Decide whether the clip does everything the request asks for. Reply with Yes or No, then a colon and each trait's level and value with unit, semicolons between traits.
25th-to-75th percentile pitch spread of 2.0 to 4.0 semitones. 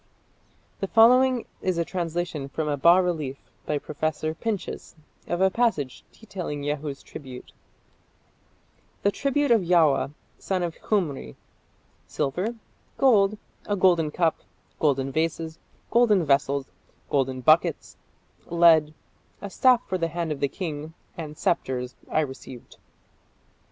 No: average, 4.6 semitones